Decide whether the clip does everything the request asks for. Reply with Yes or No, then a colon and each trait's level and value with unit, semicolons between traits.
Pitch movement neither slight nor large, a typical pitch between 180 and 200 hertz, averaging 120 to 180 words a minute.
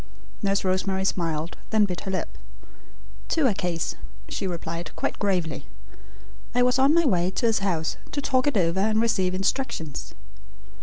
Yes: average, 4.8 semitones; high, 190 Hz; average, 160 wpm